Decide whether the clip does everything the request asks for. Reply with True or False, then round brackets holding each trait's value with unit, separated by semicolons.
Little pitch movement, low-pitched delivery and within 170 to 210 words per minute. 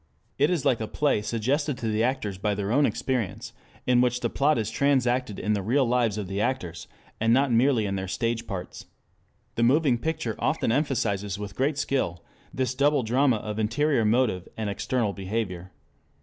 False (4.1 semitones; 115 Hz; 185 wpm)